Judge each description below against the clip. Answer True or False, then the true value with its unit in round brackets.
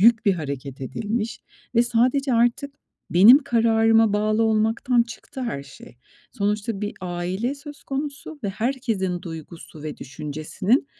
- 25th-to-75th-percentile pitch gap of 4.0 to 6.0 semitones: True (5.1 semitones)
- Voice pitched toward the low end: False (220 Hz)